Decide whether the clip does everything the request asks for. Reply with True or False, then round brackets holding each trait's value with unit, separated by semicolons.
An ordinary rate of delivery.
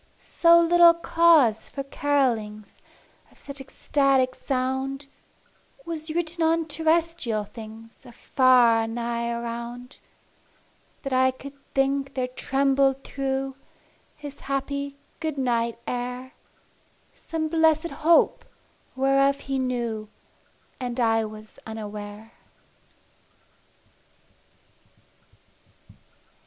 False (90 wpm)